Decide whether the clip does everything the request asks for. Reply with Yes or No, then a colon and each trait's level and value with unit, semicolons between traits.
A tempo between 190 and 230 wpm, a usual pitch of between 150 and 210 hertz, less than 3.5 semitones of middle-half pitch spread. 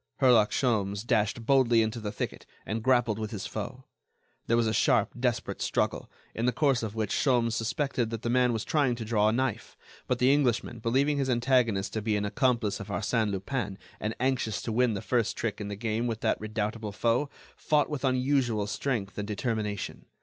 No: average, 200 wpm; low, 115 Hz; average, 2.9 semitones